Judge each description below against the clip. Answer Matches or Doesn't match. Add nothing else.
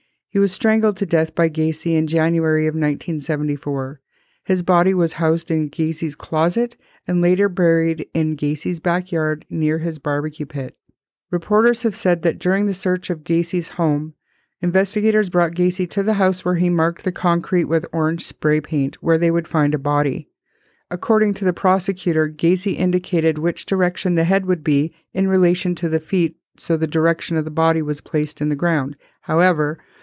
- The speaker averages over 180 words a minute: Doesn't match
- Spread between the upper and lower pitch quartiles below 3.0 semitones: Matches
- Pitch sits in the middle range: Matches